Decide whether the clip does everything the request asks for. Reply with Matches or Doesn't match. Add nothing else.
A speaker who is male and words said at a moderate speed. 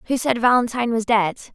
Doesn't match